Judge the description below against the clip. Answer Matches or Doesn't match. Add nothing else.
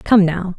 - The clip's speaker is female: Matches